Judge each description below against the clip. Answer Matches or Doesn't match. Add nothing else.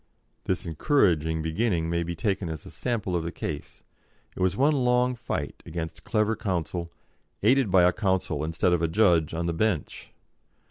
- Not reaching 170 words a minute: Doesn't match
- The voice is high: Doesn't match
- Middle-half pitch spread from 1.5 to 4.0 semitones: Doesn't match